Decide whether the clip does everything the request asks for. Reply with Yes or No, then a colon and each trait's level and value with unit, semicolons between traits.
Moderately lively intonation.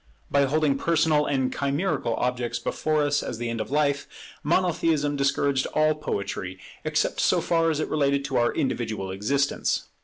Yes: average, 3.4 semitones